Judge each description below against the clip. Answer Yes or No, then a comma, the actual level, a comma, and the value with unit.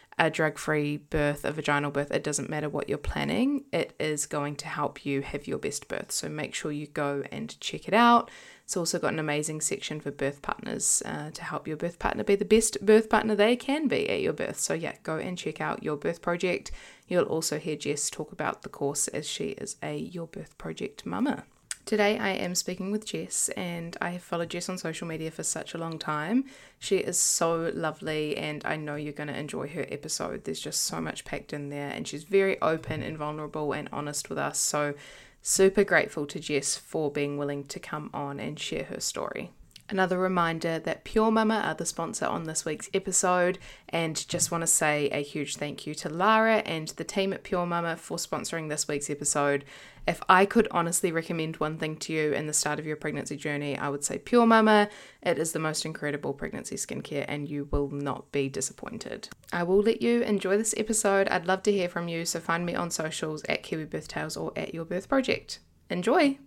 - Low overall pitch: No, medium, 160 Hz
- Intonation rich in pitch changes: No, average, 4.6 semitones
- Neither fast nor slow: No, fast, 220 wpm